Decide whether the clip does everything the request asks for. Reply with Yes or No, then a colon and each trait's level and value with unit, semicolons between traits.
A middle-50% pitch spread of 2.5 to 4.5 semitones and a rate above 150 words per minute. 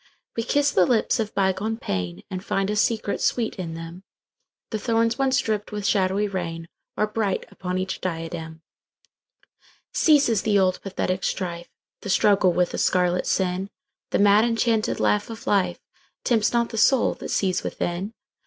No: average, 3.6 semitones; average, 140 wpm